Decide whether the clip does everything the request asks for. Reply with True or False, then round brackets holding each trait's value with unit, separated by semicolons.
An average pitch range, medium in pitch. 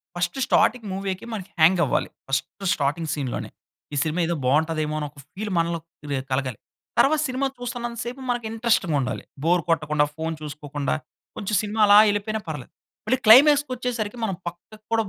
False (6.6 semitones; 180 Hz)